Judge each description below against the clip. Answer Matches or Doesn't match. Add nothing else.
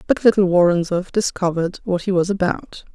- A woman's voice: Matches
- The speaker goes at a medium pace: Matches